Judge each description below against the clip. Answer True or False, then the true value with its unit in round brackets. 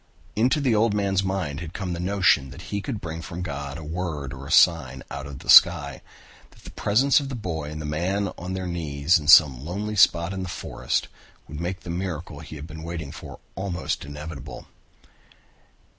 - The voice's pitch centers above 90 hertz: False (85 Hz)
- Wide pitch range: False (4.3 semitones)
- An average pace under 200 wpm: False (205 wpm)